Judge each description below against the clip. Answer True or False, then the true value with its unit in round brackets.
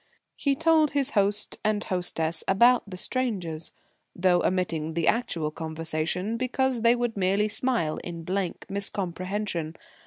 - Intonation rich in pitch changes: True (5.8 semitones)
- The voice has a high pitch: True (195 Hz)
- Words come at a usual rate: False (130 wpm)